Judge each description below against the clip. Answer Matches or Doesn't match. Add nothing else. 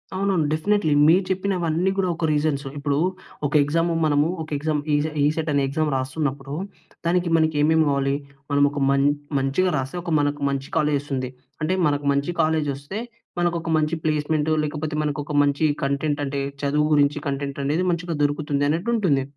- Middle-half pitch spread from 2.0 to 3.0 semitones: Matches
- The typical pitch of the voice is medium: Matches